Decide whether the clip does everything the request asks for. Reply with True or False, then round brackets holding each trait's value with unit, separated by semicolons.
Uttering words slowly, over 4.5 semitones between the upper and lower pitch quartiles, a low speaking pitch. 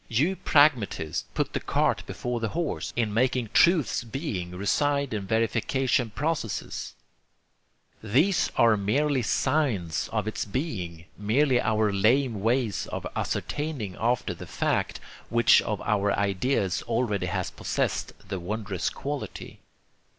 True (125 wpm; 5.0 semitones; 115 Hz)